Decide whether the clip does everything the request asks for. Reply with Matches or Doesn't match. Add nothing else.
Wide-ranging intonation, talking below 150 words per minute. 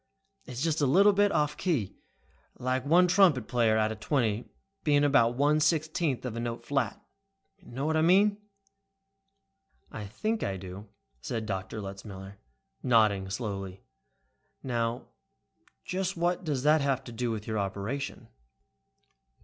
Matches